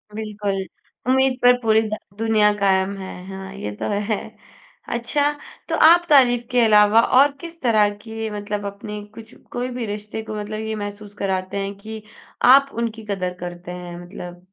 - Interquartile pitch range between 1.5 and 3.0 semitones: Yes, narrow, 2.6 semitones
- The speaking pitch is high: Yes, high, 210 Hz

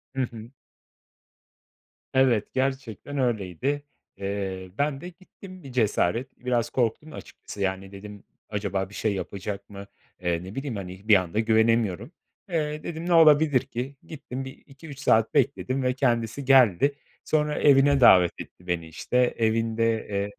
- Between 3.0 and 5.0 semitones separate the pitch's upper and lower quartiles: No, wide, 5.4 semitones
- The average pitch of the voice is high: No, low, 115 Hz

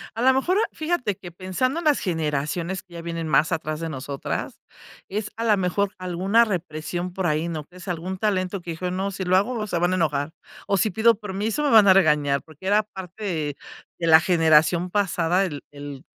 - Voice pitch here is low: No, medium, 180 Hz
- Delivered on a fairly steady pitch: No, average, 3.9 semitones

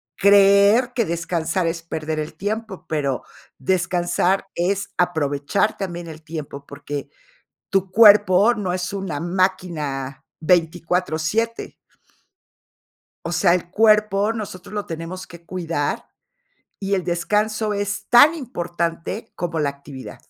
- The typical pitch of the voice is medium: Yes, medium, 180 Hz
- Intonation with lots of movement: No, average, 3.7 semitones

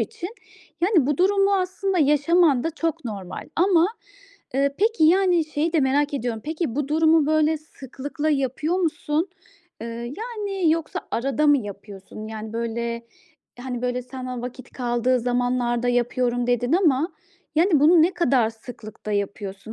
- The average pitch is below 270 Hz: No, very high, 280 Hz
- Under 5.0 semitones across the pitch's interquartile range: No, average, 5.3 semitones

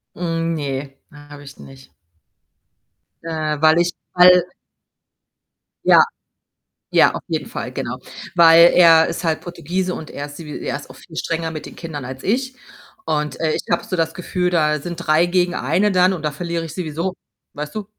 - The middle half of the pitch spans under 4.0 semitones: Yes, average, 2.9 semitones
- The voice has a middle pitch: Yes, medium, 165 Hz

